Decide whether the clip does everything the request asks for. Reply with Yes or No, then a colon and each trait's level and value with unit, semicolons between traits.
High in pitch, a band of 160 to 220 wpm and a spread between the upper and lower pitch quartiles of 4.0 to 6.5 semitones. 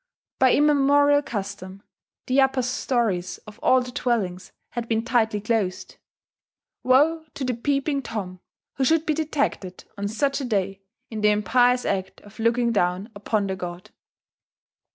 No: high, 230 Hz; average, 150 wpm; average, 5.0 semitones